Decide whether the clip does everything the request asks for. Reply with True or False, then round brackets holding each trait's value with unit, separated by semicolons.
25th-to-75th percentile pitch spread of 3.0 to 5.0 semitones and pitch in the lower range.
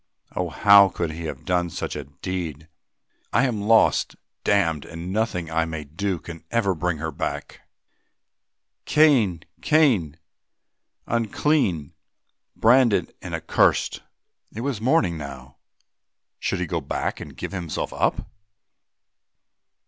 False (5.4 semitones; 90 Hz)